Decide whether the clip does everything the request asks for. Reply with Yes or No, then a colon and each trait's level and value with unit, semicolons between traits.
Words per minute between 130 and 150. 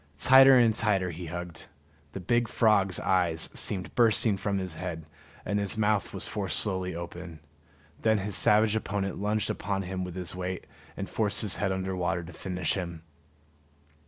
No: average, 170 wpm